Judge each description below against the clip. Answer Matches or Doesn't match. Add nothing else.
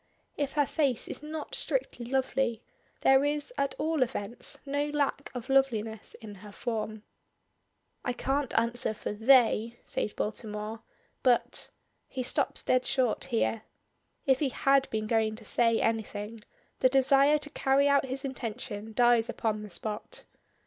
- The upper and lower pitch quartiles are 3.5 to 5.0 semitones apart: Matches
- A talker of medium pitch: Doesn't match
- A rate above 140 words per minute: Matches